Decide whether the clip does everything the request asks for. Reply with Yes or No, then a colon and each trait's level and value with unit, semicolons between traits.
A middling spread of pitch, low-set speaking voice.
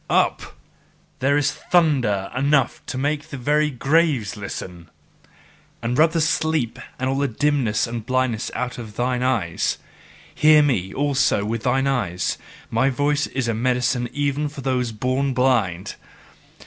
Yes: average, 3.7 semitones; low, 130 Hz